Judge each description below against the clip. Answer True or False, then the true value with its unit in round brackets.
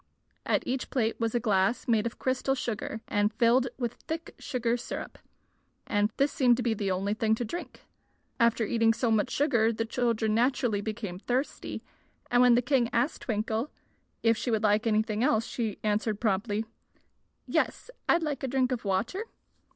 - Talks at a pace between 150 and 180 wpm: True (175 wpm)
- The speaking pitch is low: False (230 Hz)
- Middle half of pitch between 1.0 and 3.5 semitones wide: True (2.6 semitones)